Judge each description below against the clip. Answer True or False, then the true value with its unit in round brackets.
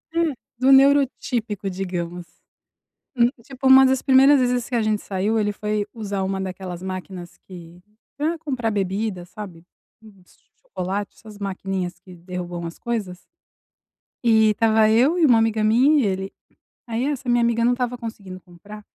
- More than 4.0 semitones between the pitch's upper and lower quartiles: True (4.7 semitones)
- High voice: True (215 Hz)